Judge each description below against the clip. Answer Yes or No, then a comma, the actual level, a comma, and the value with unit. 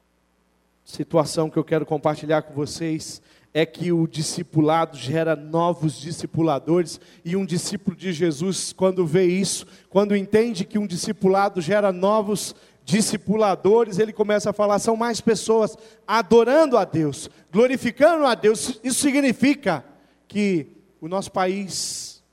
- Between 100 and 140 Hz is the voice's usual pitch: No, medium, 185 Hz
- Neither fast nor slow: Yes, average, 130 wpm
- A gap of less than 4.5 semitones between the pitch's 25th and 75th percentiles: No, average, 5.0 semitones